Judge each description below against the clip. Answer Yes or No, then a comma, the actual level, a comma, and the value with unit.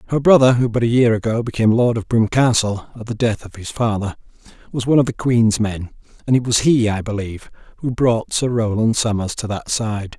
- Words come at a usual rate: No, fast, 220 wpm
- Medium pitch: No, low, 115 Hz